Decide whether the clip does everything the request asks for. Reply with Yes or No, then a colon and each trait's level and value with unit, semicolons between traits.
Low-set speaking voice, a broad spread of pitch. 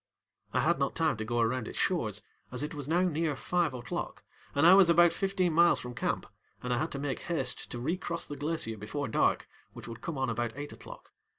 No: medium, 145 Hz; wide, 5.9 semitones